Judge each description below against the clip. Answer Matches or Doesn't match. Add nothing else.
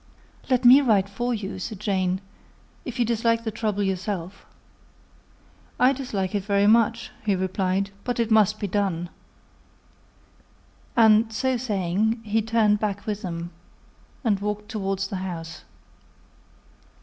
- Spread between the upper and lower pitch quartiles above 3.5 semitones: Doesn't match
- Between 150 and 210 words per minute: Doesn't match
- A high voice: Matches